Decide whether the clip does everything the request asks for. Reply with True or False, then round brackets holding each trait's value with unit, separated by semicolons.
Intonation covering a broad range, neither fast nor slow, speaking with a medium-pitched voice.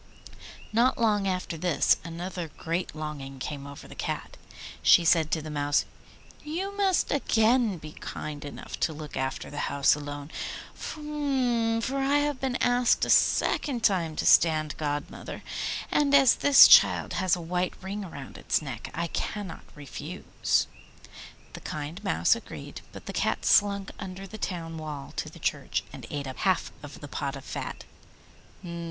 True (7.4 semitones; 160 wpm; 175 Hz)